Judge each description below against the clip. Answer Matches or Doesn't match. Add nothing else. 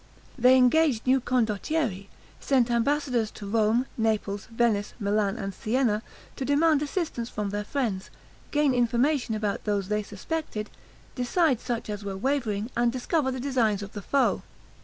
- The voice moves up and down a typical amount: Matches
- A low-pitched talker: Doesn't match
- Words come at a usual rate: Matches